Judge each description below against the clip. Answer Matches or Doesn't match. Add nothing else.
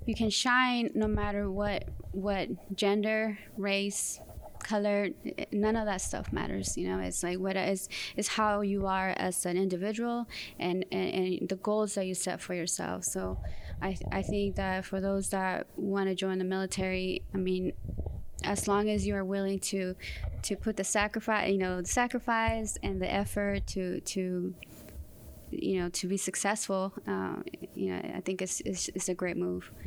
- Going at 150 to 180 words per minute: Matches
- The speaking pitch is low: Doesn't match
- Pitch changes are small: Matches